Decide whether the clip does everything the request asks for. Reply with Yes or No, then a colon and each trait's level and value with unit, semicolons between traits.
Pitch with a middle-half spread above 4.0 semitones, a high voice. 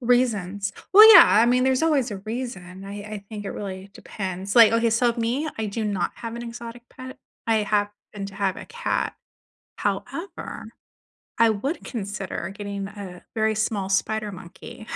No: average, 3.1 semitones; high, 215 Hz